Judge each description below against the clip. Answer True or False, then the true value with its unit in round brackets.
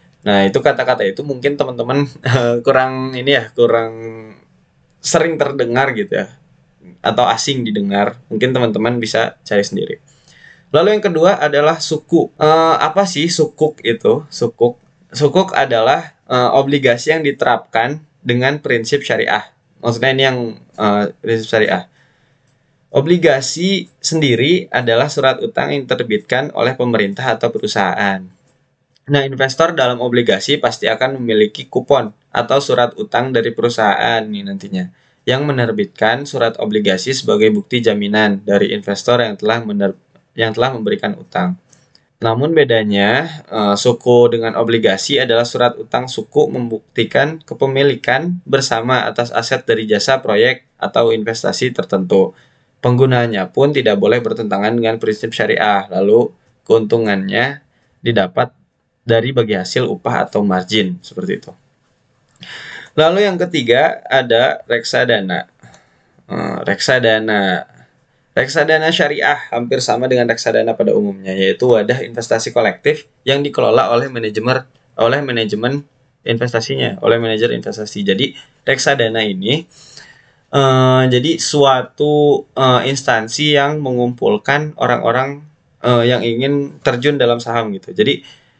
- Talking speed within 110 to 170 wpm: True (120 wpm)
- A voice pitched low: True (125 Hz)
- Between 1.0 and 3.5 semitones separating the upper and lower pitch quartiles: False (4.2 semitones)